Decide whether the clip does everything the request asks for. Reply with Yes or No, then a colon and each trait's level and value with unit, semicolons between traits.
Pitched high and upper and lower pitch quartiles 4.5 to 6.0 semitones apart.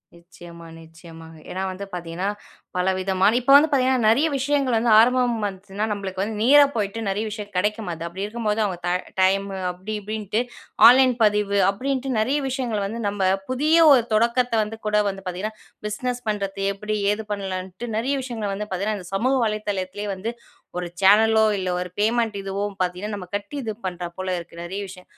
No: high, 210 Hz; average, 3.5 semitones